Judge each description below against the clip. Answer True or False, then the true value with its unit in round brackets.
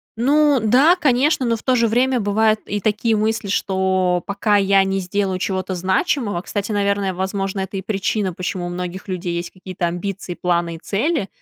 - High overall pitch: True (200 Hz)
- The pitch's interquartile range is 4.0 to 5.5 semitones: False (3.0 semitones)